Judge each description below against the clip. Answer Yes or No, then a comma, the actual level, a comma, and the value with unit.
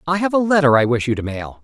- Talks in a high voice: No, medium, 150 Hz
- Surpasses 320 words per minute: Yes, fast, 330 wpm